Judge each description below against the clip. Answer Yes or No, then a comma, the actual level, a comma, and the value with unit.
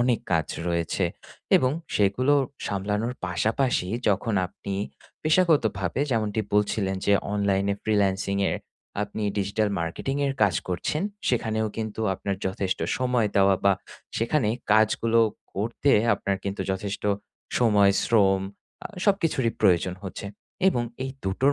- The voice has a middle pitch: No, low, 105 Hz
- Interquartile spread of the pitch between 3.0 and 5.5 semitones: Yes, average, 3.3 semitones